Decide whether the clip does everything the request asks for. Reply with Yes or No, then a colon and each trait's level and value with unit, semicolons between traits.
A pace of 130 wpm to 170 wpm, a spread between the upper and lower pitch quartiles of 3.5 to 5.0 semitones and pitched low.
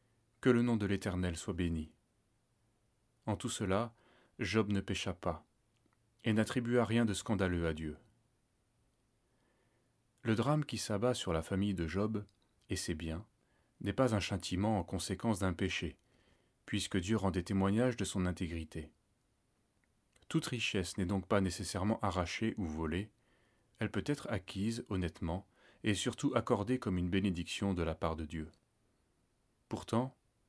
Yes: average, 150 wpm; average, 3.9 semitones; low, 105 Hz